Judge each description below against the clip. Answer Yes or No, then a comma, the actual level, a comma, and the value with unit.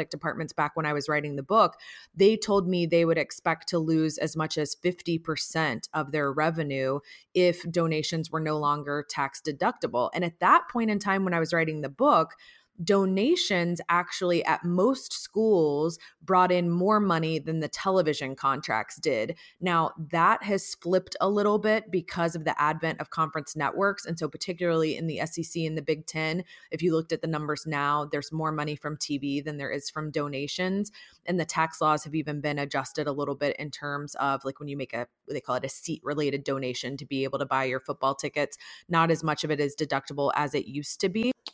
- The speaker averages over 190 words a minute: Yes, fast, 205 wpm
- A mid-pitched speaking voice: Yes, medium, 155 Hz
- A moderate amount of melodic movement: Yes, average, 3.1 semitones